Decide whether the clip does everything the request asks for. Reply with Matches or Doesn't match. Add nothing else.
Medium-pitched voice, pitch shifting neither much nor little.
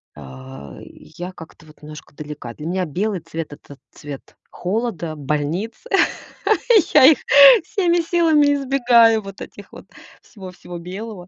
Doesn't match